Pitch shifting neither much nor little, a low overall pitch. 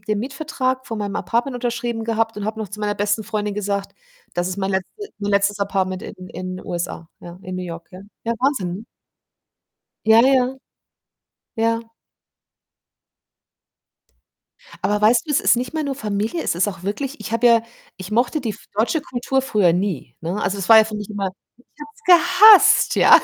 No: average, 3.7 semitones; high, 215 Hz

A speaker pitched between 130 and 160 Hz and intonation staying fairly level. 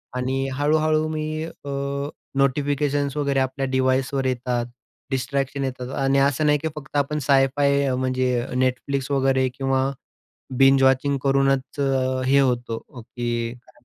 Yes: low, 135 Hz; narrow, 1.5 semitones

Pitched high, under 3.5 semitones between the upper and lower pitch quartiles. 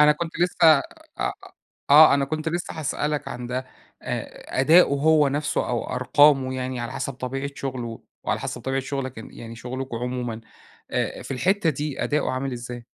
No: low, 135 Hz; average, 3.0 semitones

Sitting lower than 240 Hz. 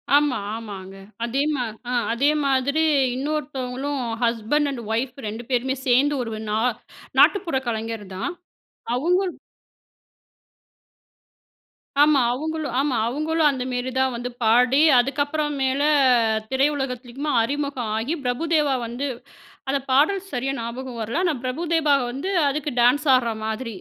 No: very high, 265 Hz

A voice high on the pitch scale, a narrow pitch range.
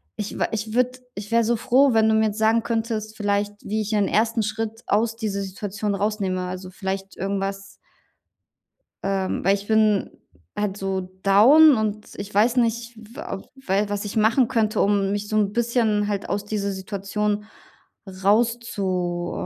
Yes: high, 210 Hz; narrow, 2.2 semitones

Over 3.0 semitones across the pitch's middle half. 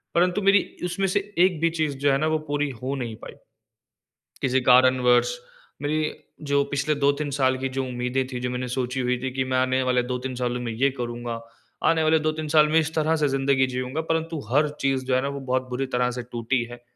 Yes: average, 3.4 semitones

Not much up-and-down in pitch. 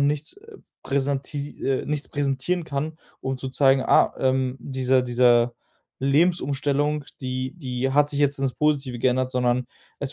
Yes: narrow, 2.1 semitones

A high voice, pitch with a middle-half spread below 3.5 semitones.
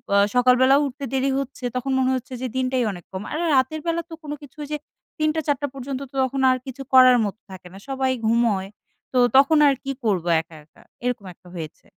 Yes: very high, 260 Hz; average, 2.9 semitones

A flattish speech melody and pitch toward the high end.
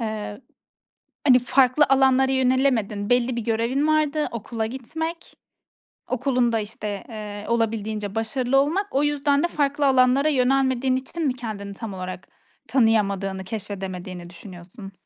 No: average, 4.4 semitones; high, 240 Hz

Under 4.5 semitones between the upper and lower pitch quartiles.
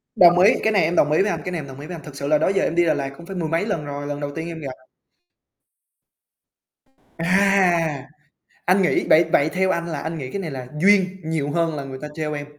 Yes: average, 3.8 semitones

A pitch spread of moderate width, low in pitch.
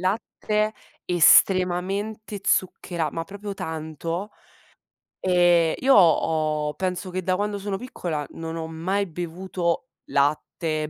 No: average, 3.4 semitones; medium, 180 Hz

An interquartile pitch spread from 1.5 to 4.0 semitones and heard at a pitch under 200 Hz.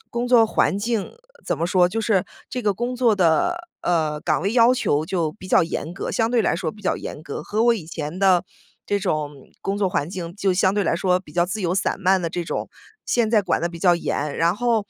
No: average, 4.4 semitones; medium, 185 Hz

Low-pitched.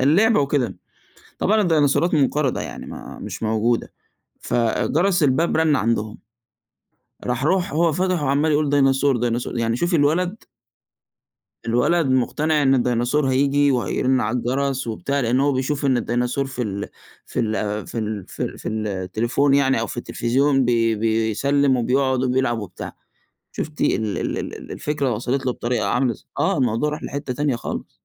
Yes: low, 130 Hz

